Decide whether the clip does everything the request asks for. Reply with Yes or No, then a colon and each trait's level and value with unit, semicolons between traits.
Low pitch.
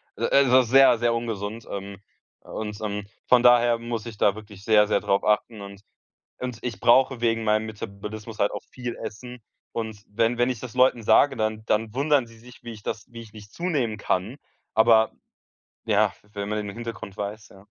Yes: low, 110 Hz